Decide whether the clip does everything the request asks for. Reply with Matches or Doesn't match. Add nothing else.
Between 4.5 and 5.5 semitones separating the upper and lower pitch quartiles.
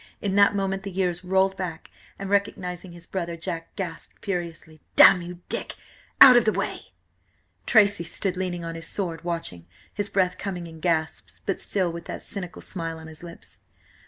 Doesn't match